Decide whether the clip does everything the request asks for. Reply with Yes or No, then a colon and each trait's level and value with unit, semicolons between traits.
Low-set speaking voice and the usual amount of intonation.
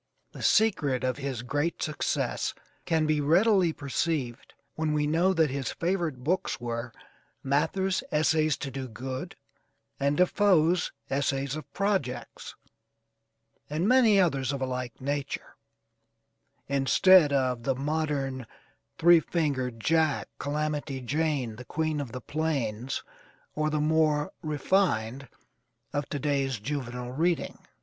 No: medium, 145 Hz; average, 3.4 semitones